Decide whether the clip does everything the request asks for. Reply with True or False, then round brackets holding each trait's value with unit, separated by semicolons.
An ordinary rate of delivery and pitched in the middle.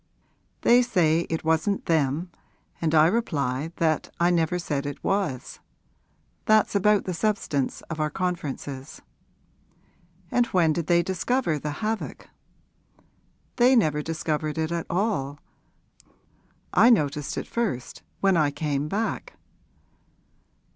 False (120 wpm; 165 Hz)